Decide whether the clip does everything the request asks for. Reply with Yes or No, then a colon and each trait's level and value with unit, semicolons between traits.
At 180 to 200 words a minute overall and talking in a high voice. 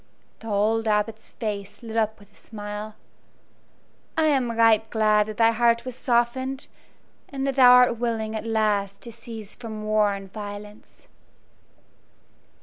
No: average, 145 wpm; high, 220 Hz